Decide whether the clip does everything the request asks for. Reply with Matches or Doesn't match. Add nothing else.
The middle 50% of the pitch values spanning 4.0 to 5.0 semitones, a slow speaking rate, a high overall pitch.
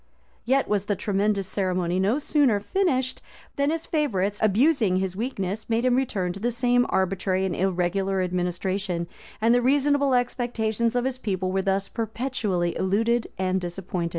Doesn't match